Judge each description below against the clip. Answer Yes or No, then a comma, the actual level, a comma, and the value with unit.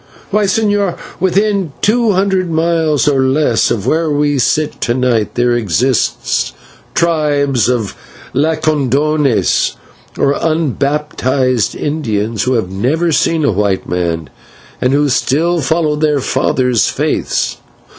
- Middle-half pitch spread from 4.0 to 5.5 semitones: Yes, average, 4.6 semitones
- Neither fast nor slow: No, slow, 120 wpm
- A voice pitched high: No, medium, 145 Hz